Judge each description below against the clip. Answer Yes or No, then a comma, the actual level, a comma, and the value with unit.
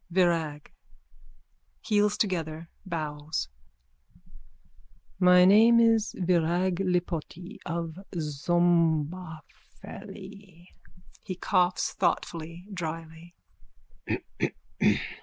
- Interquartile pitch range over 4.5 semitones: No, narrow, 2.5 semitones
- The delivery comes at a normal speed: No, slow, 65 wpm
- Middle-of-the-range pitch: Yes, medium, 175 Hz